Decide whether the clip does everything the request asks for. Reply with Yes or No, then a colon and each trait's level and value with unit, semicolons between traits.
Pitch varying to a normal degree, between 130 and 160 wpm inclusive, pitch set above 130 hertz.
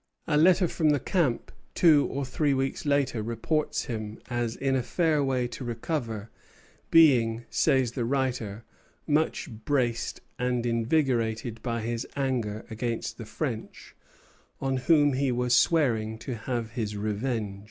No: average, 3.7 semitones; average, 140 wpm; low, 125 Hz